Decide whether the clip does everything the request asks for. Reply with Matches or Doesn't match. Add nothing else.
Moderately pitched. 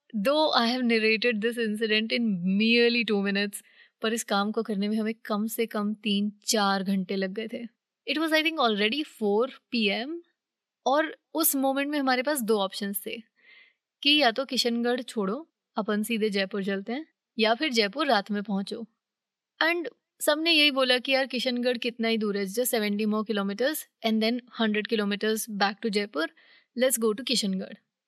Doesn't match